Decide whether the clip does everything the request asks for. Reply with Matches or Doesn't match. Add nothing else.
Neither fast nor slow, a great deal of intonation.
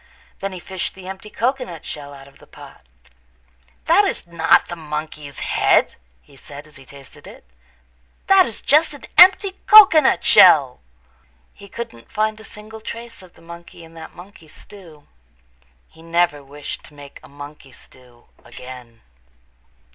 Matches